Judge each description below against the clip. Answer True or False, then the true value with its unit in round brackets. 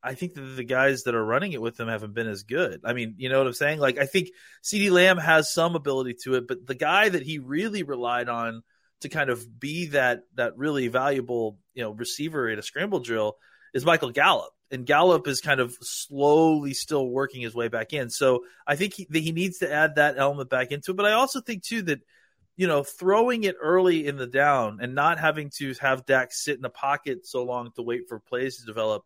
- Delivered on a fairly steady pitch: False (4.6 semitones)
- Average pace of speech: False (240 wpm)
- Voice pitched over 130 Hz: True (140 Hz)